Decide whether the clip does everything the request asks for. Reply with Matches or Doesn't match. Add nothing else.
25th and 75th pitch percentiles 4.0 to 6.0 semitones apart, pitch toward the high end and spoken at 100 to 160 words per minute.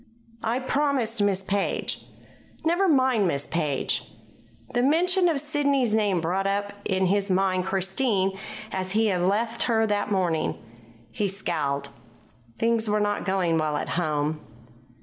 Matches